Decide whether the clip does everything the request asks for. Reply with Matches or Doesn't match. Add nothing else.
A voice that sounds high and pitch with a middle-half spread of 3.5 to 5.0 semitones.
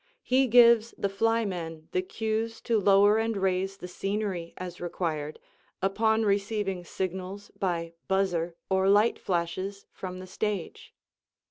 Doesn't match